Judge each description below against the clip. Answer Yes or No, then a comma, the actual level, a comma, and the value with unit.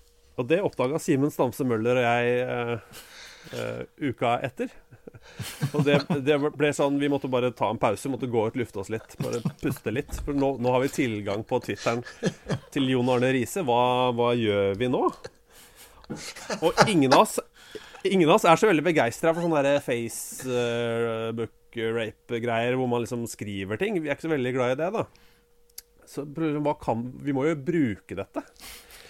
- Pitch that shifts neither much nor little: Yes, average, 3.5 semitones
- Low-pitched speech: Yes, low, 125 Hz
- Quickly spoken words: No, average, 175 wpm